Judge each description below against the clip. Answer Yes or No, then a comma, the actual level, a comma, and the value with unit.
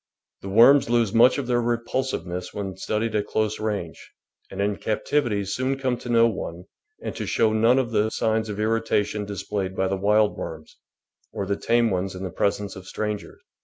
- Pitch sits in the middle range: No, low, 105 Hz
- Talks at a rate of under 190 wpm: No, average, 195 wpm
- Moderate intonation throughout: Yes, average, 3.0 semitones